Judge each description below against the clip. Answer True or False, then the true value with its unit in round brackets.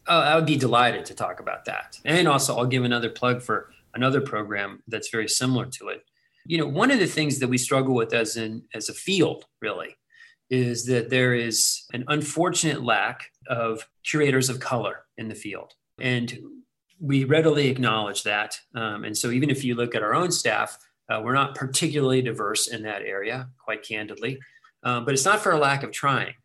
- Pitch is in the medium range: False (130 Hz)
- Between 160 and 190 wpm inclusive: False (200 wpm)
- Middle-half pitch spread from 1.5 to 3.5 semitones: False (4.3 semitones)